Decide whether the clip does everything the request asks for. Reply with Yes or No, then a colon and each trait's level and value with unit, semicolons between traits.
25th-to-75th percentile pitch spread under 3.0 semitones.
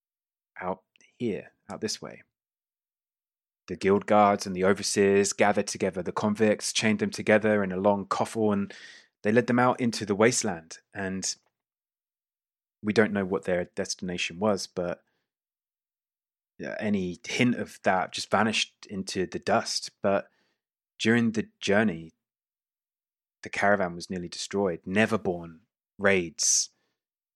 Yes: narrow, 2.5 semitones